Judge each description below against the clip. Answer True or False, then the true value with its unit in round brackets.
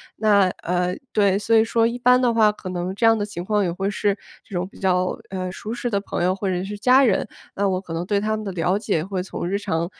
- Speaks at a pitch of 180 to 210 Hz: True (200 Hz)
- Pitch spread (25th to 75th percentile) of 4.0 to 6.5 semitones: False (2.8 semitones)